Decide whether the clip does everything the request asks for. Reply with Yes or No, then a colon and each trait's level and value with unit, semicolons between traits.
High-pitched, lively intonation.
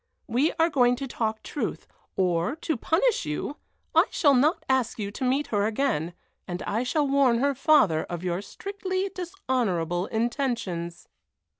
Yes: high, 245 Hz; wide, 7.0 semitones